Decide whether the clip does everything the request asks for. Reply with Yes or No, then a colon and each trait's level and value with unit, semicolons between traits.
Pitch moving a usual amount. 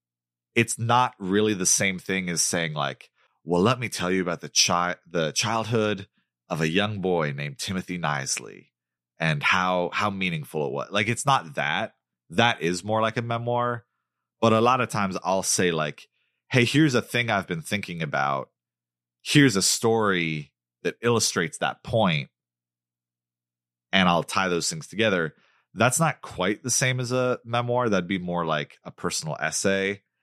No: wide, 7.1 semitones